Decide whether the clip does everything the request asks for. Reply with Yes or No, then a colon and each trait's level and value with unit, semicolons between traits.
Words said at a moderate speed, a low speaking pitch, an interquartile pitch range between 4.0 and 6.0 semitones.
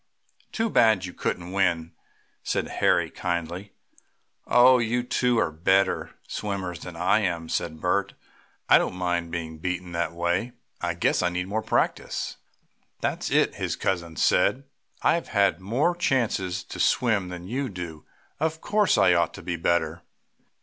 Yes: average, 160 wpm; very low, 90 Hz; average, 4.4 semitones